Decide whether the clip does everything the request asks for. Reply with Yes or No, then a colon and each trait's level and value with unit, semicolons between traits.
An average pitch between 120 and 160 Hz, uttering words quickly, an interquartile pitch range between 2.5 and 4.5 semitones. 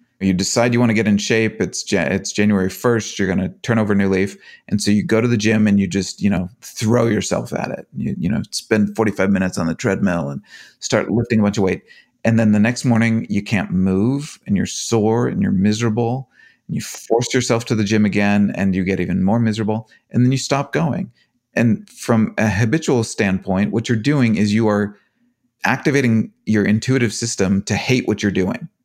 No: low, 110 Hz; fast, 220 wpm; average, 2.9 semitones